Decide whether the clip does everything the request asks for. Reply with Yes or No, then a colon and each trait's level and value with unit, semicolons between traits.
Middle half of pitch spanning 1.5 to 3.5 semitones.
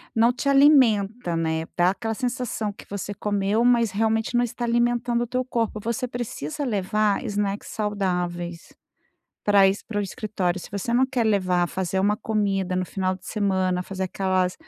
No: average, 3.9 semitones